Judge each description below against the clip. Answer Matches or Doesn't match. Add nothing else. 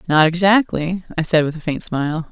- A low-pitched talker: Doesn't match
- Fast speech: Matches